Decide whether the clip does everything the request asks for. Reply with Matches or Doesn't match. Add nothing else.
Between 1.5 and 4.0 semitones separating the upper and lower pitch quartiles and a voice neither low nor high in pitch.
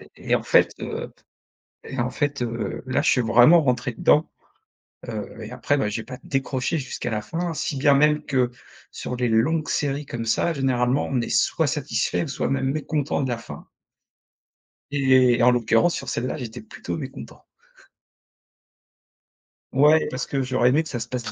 Doesn't match